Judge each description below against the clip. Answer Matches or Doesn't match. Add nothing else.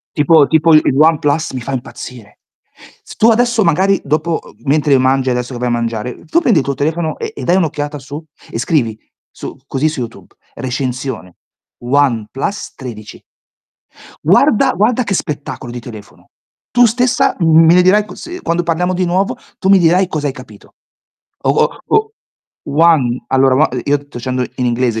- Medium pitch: Matches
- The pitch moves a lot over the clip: Matches